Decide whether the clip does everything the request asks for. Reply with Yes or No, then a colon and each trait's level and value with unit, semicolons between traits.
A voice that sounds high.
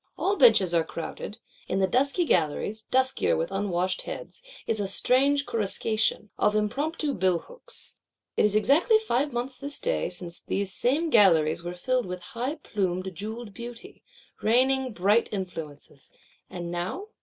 Yes: high, 215 Hz